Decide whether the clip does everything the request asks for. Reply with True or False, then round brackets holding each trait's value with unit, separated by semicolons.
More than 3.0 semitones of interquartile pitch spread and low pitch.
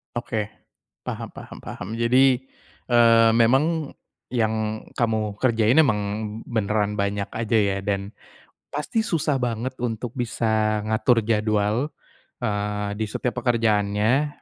False (2.7 semitones; 110 Hz)